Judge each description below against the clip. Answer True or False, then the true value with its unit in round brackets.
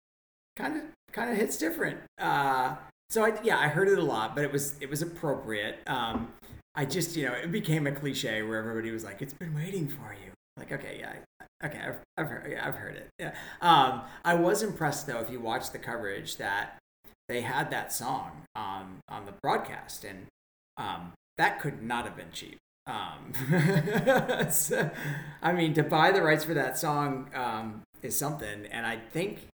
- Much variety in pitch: True (6.4 semitones)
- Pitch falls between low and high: True (145 Hz)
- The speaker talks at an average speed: True (195 wpm)